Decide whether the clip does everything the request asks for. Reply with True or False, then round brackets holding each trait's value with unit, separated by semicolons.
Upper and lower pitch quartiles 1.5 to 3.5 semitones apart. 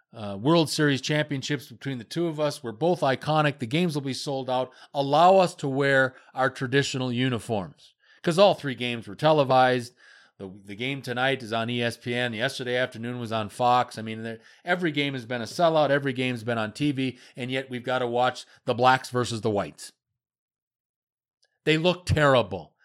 True (2.9 semitones)